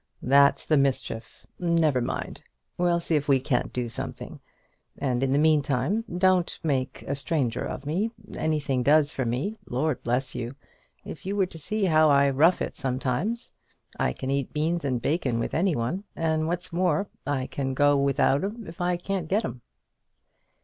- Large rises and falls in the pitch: No, average, 4.6 semitones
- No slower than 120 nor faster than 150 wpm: No, average, 175 wpm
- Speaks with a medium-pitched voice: Yes, medium, 145 Hz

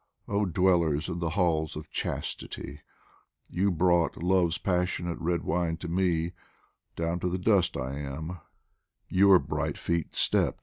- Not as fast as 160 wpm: Yes, average, 140 wpm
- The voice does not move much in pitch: Yes, narrow, 2.0 semitones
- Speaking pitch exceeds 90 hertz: No, very low, 85 Hz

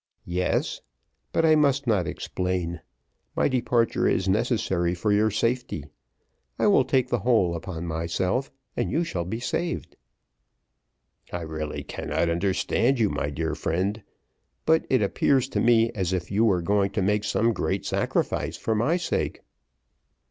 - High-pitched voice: No, low, 105 Hz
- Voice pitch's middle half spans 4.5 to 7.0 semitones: Yes, wide, 5.6 semitones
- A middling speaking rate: Yes, average, 150 wpm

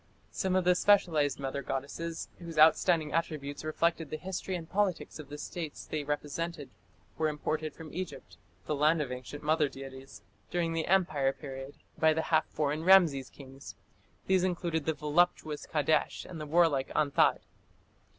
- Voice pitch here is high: No, medium, 155 Hz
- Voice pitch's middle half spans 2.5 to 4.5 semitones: Yes, average, 2.9 semitones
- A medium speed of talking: Yes, average, 160 wpm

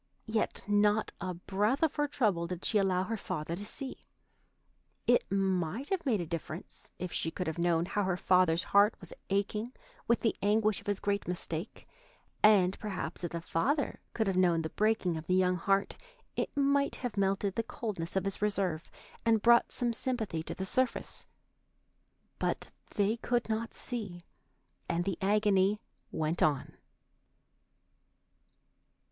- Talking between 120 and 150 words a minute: No, average, 160 wpm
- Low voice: No, high, 195 Hz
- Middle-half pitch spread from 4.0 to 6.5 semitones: No, average, 3.6 semitones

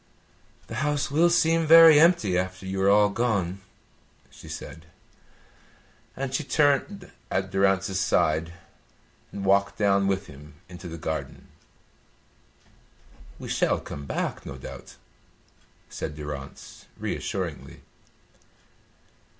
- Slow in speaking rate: Yes, slow, 110 wpm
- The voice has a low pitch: Yes, low, 100 Hz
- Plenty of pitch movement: Yes, wide, 8.4 semitones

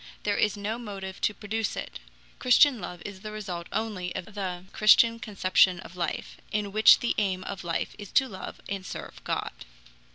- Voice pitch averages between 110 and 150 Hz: No, high, 205 Hz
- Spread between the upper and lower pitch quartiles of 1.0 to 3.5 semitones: Yes, average, 2.7 semitones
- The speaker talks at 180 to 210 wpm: Yes, average, 185 wpm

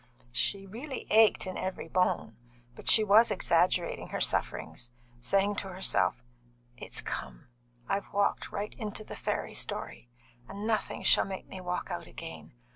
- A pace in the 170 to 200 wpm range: No, average, 150 wpm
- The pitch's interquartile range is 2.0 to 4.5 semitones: Yes, average, 2.9 semitones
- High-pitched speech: Yes, high, 195 Hz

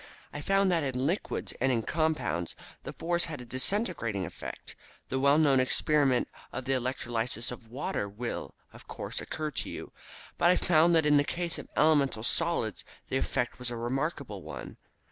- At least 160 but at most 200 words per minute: Yes, average, 180 wpm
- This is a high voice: No, low, 135 Hz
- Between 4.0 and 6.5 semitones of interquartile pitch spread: Yes, average, 4.9 semitones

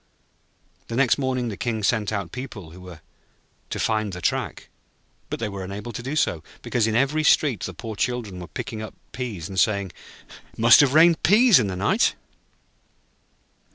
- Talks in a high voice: No, low, 110 Hz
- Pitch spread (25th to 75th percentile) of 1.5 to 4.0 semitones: No, average, 4.5 semitones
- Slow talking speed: No, average, 185 wpm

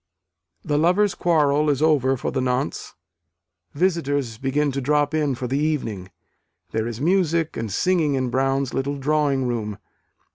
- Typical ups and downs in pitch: Yes, average, 3.1 semitones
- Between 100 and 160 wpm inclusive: Yes, average, 150 wpm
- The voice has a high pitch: No, medium, 140 Hz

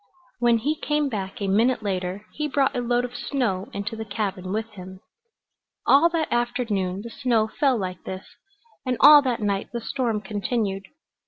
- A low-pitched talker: No, high, 225 Hz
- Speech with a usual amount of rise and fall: Yes, average, 4.2 semitones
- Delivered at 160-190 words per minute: Yes, average, 175 wpm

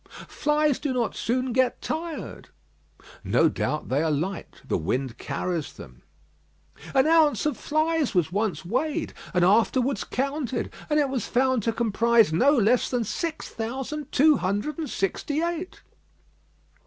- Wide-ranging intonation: Yes, wide, 6.6 semitones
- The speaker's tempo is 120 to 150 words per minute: Yes, average, 145 wpm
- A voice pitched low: No, very high, 255 Hz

